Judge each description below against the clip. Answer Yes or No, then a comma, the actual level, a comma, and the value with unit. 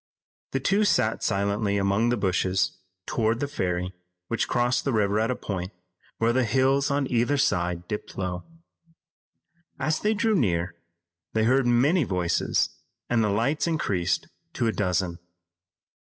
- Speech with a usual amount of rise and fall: No, wide, 5.7 semitones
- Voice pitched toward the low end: Yes, low, 110 Hz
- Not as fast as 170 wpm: Yes, average, 150 wpm